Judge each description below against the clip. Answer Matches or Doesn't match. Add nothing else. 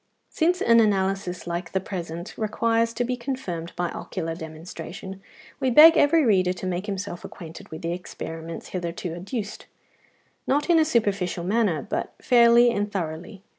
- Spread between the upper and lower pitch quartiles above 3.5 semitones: Matches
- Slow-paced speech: Doesn't match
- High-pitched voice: Matches